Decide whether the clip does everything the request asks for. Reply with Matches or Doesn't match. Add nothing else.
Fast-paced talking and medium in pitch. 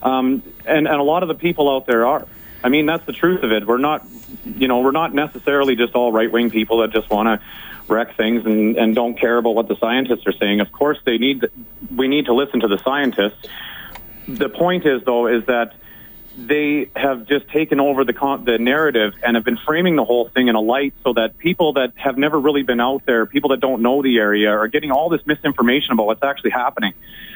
Doesn't match